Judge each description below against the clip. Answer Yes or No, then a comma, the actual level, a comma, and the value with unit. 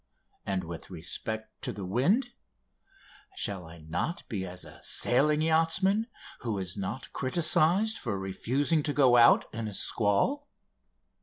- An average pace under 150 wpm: Yes, average, 140 wpm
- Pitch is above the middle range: No, low, 120 Hz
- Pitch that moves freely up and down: Yes, wide, 8.9 semitones